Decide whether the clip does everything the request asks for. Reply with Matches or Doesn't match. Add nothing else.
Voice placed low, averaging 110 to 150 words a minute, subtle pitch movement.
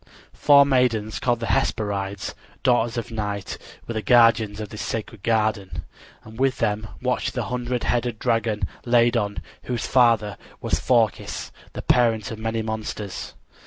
Matches